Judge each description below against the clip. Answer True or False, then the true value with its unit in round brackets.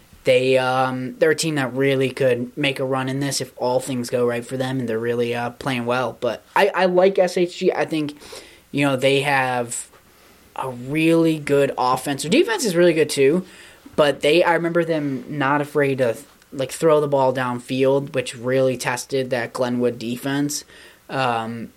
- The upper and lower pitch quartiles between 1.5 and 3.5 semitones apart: True (2.7 semitones)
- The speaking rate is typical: True (185 wpm)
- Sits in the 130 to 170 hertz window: True (135 Hz)